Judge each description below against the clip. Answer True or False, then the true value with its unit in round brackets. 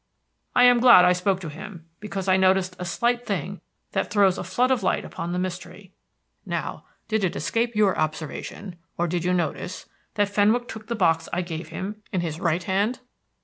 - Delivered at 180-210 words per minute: True (195 wpm)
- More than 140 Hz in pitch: True (185 Hz)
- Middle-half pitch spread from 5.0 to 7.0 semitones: False (3.3 semitones)